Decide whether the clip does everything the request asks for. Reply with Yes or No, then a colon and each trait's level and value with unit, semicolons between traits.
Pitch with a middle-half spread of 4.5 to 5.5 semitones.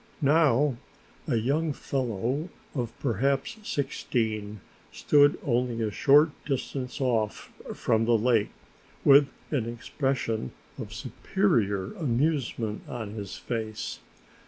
No: average, 4.1 semitones